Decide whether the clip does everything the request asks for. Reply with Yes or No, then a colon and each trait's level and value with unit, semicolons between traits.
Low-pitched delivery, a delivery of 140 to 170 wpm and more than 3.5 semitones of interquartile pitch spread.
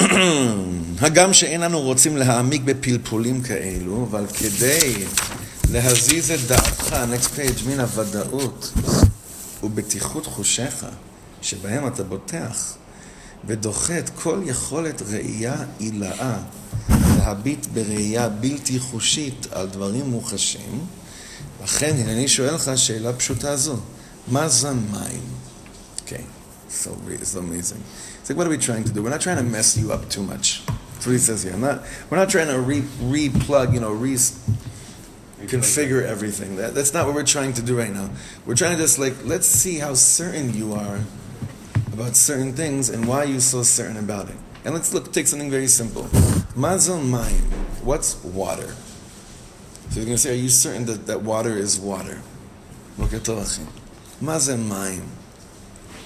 Yes: low, 120 Hz; average, 150 wpm; average, 4.6 semitones